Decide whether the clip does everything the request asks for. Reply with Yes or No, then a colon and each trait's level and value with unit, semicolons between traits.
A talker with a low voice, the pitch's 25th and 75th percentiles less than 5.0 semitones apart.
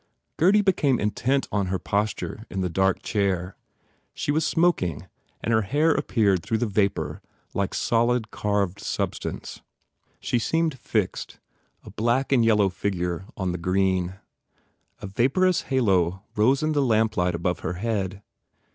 No: low, 105 Hz; wide, 5.4 semitones